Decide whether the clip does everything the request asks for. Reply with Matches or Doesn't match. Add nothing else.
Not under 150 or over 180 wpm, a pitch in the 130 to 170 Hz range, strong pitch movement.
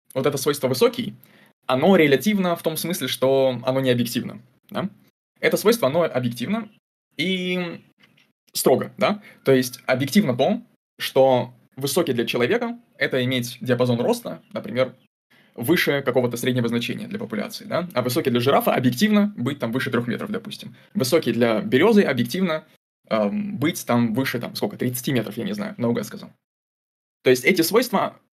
Matches